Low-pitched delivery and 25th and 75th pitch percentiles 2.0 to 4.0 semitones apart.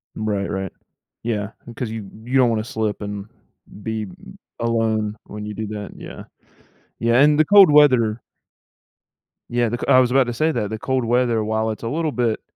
Yes: low, 115 Hz; average, 2.7 semitones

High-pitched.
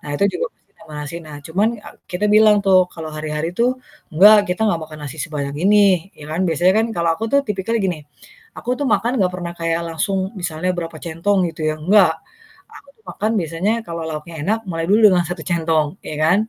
No: medium, 175 Hz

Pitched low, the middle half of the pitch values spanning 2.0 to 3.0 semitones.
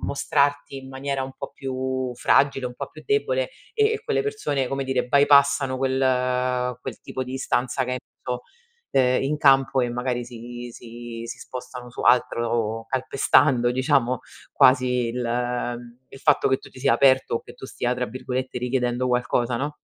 No: low, 130 Hz; narrow, 1.6 semitones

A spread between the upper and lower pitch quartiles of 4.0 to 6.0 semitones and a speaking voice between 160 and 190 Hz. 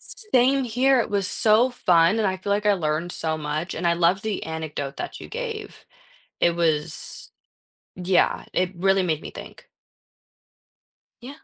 Yes: average, 5.1 semitones; medium, 185 Hz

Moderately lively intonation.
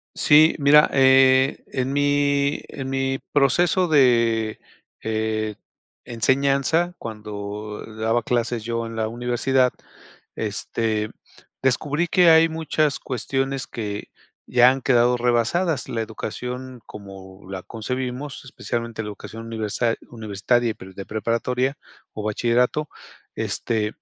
Yes: average, 3.6 semitones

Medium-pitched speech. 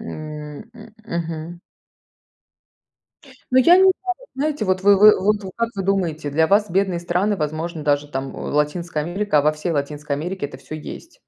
Yes: medium, 170 Hz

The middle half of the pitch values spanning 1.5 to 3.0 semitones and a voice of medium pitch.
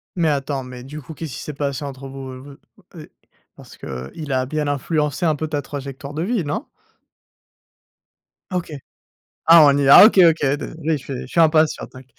Yes: average, 2.7 semitones; medium, 145 Hz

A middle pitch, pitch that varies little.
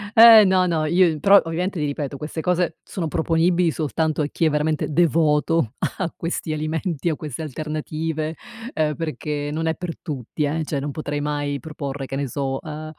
Yes: medium, 155 Hz; narrow, 2.0 semitones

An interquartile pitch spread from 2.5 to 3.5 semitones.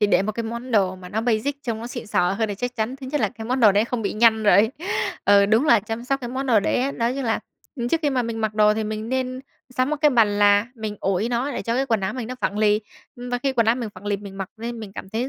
Yes: average, 3.0 semitones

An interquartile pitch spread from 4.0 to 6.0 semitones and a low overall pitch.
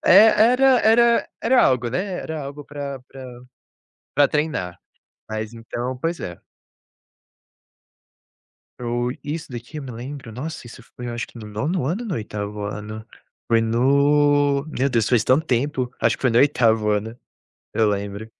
Yes: average, 4.6 semitones; low, 130 Hz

